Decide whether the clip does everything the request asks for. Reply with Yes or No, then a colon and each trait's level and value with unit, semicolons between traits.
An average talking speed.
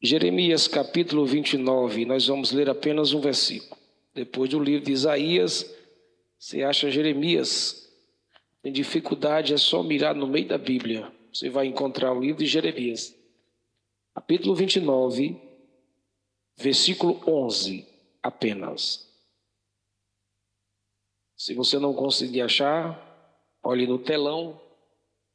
No: slow, 110 wpm